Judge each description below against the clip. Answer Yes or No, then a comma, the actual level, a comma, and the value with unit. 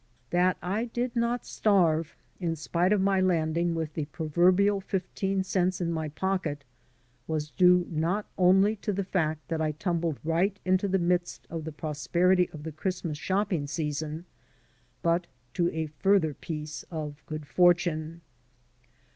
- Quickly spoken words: No, average, 155 wpm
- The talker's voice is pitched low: No, medium, 175 Hz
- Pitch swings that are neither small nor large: Yes, average, 3.1 semitones